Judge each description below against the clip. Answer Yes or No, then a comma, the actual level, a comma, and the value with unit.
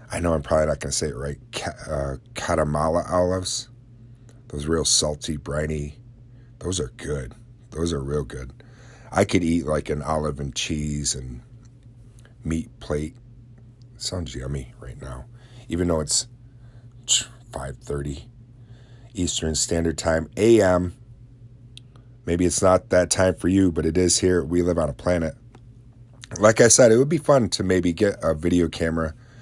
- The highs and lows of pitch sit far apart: Yes, wide, 6.9 semitones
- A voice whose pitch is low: Yes, very low, 90 Hz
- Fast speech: No, average, 155 wpm